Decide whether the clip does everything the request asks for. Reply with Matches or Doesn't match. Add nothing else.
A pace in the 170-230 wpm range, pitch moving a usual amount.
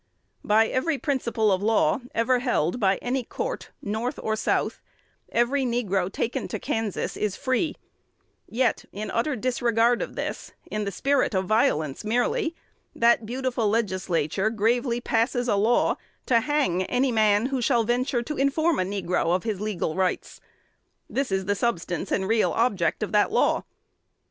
Doesn't match